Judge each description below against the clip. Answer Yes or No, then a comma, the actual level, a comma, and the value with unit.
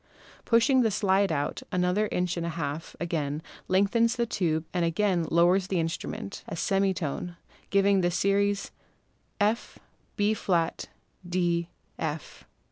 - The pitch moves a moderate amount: Yes, average, 3.2 semitones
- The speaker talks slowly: Yes, slow, 130 wpm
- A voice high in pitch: No, medium, 180 Hz